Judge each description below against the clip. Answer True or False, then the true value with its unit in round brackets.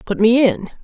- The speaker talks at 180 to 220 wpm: True (215 wpm)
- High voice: True (230 Hz)